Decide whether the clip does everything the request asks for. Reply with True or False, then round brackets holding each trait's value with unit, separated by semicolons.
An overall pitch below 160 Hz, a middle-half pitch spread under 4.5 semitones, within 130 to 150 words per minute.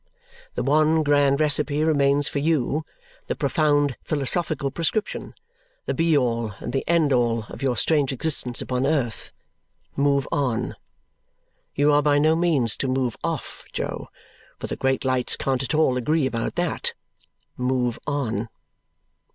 True (140 Hz; 3.3 semitones; 145 wpm)